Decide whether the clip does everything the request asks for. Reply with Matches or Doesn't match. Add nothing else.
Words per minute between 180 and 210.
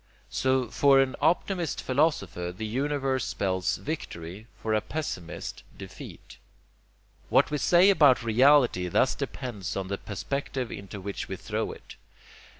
Doesn't match